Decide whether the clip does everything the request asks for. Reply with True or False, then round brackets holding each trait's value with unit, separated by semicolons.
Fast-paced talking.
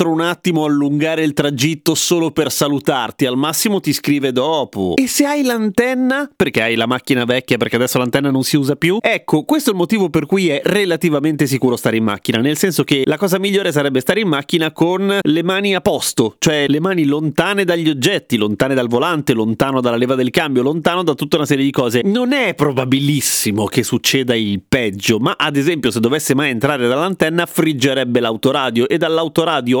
True (195 wpm)